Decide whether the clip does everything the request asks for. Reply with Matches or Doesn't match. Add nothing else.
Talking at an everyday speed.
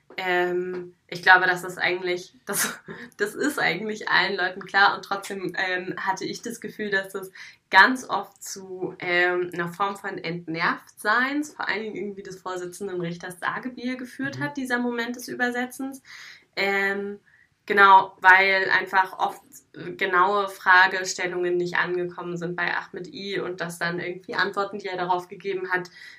Matches